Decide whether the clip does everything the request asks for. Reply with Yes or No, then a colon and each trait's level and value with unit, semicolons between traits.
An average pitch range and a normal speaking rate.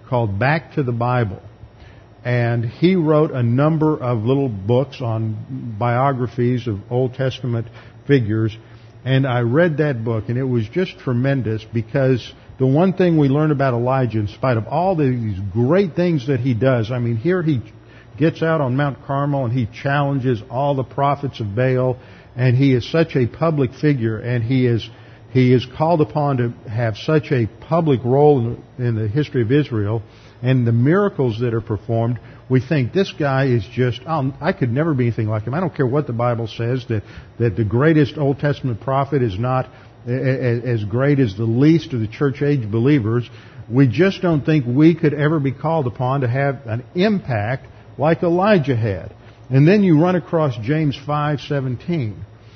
Yes: average, 3.8 semitones; average, 185 wpm